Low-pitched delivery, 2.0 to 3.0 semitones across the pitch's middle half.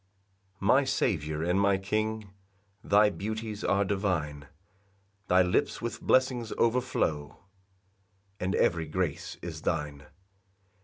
No: low, 100 Hz; average, 4.7 semitones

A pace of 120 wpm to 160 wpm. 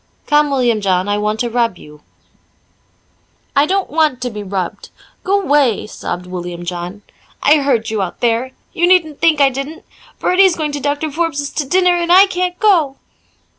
No: average, 170 wpm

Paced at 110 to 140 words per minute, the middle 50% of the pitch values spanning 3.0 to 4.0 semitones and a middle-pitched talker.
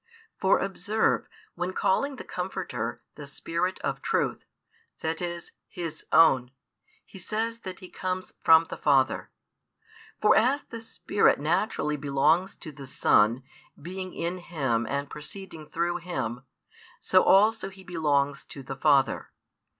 No: slow, 135 wpm; average, 5.0 semitones; medium, 170 Hz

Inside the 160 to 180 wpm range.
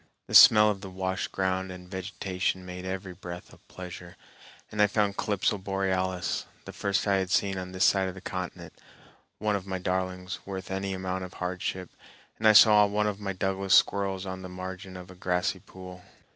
No: average, 195 wpm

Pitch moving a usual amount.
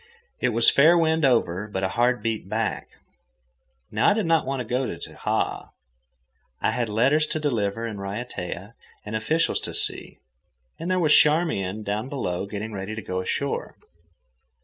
No: wide, 6.4 semitones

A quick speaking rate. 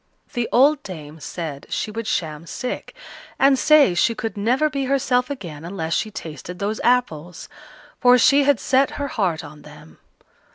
No: average, 165 wpm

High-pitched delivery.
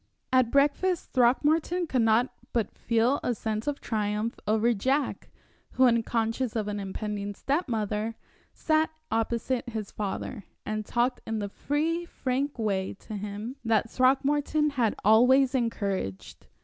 Yes: high, 235 Hz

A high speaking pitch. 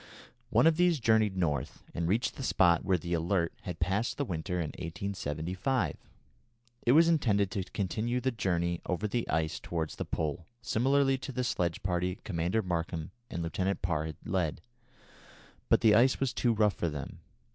No: very low, 95 Hz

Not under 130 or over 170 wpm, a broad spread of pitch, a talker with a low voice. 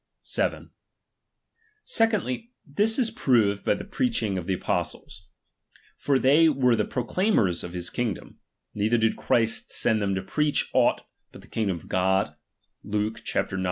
Yes: average, 155 wpm; wide, 7.3 semitones; low, 115 Hz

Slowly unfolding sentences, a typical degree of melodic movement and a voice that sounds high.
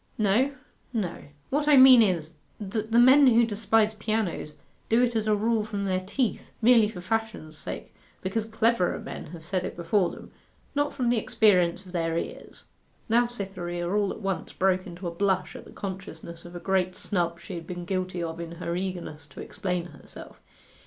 No: average, 190 wpm; average, 4.2 semitones; high, 195 Hz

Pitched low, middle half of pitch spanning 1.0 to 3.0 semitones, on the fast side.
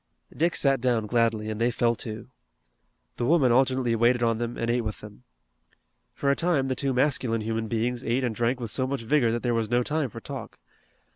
Yes: low, 120 Hz; narrow, 2.4 semitones; fast, 215 wpm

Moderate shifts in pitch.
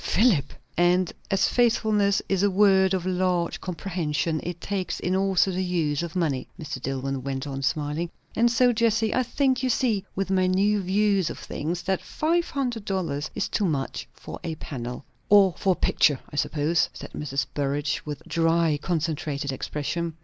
Yes: average, 4.9 semitones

